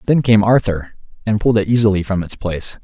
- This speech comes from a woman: No, male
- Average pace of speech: No, fast, 210 wpm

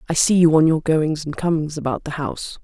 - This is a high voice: No, medium, 155 Hz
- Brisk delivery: Yes, fast, 250 wpm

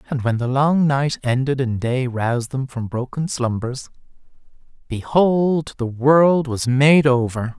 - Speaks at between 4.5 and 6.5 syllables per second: No, 3.9 syllables/s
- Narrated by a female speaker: No, male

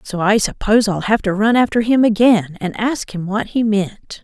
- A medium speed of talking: No, fast, 225 wpm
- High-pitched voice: Yes, high, 210 Hz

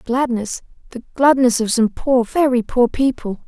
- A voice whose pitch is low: No, high, 245 Hz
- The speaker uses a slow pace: No, average, 155 wpm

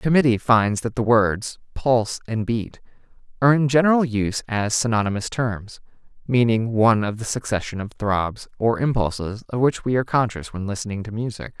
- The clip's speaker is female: No, male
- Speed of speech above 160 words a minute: Yes, average, 175 wpm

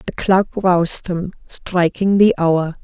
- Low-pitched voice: No, medium, 180 Hz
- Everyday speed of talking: Yes, average, 150 wpm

